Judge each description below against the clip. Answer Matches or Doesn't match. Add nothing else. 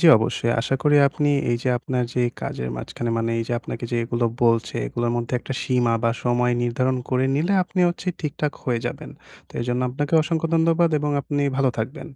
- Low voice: Matches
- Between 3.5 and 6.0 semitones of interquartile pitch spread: Matches